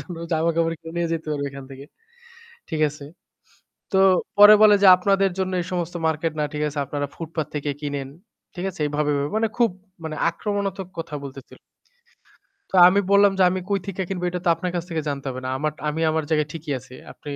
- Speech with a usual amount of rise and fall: Yes, average, 4.1 semitones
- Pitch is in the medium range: Yes, medium, 165 Hz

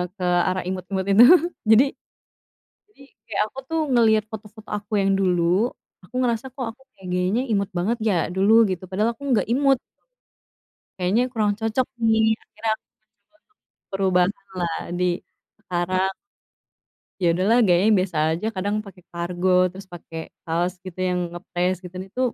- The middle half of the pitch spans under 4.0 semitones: Yes, average, 3.5 semitones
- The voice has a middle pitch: No, high, 195 Hz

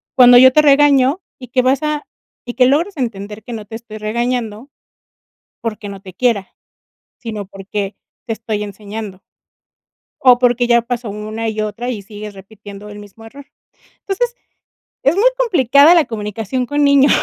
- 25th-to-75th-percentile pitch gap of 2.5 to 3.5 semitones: No, average, 3.9 semitones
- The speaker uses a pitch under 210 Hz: No, high, 235 Hz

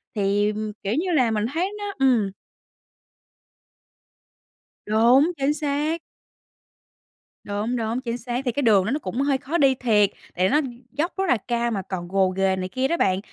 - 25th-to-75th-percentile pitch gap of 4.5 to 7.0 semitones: Yes, wide, 5.6 semitones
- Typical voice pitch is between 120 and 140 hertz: No, high, 240 Hz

